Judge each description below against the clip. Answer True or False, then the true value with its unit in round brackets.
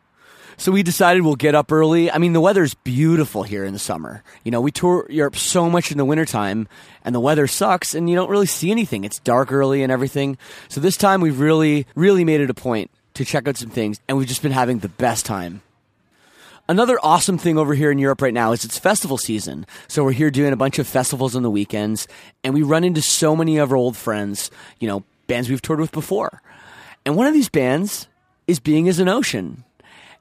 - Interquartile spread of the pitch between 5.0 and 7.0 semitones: True (5.5 semitones)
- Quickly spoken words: True (230 wpm)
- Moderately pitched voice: True (145 Hz)